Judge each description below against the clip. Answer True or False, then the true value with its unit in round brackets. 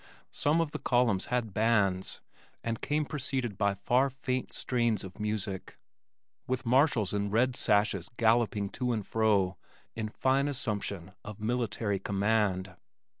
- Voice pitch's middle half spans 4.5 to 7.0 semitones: False (3.8 semitones)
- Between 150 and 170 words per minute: False (135 wpm)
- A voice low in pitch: True (110 Hz)